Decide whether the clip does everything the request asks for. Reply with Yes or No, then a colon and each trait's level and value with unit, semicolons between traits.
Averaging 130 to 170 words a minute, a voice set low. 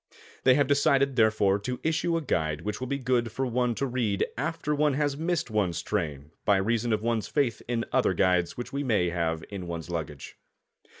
No: average, 200 wpm; low, 115 Hz